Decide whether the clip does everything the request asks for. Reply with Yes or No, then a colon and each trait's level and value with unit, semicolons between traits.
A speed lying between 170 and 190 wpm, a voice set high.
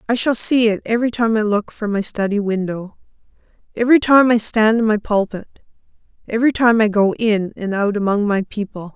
Yes: average, 180 wpm; high, 215 Hz